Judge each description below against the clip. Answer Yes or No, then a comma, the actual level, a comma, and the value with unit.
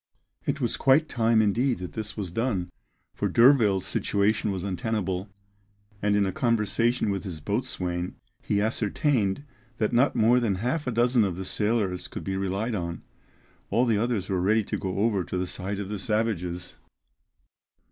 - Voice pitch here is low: Yes, low, 105 Hz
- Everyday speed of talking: Yes, average, 170 wpm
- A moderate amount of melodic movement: Yes, average, 3.4 semitones